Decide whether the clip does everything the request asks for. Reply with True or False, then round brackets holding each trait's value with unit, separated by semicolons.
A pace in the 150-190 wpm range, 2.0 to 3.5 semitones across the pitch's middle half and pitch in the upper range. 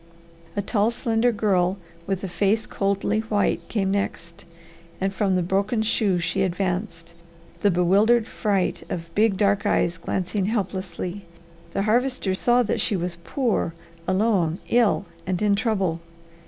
False (140 wpm; 3.0 semitones; 195 Hz)